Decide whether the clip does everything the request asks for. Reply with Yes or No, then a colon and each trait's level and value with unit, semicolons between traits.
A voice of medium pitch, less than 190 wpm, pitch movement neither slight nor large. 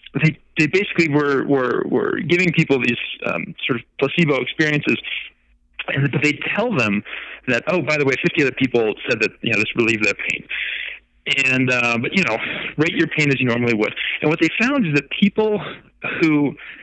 No: medium, 145 Hz; average, 200 wpm; average, 4.5 semitones